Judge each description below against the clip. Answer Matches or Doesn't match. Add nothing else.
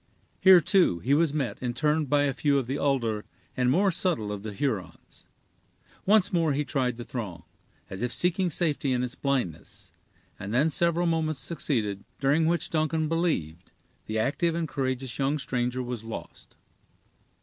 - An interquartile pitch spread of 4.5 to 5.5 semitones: Matches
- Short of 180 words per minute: Matches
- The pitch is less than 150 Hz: Matches